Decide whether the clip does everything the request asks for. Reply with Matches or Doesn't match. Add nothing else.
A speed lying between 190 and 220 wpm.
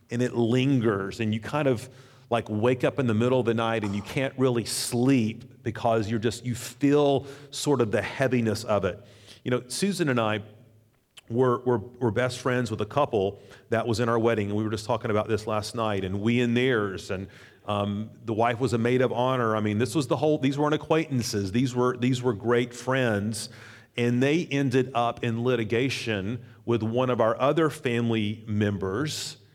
Matches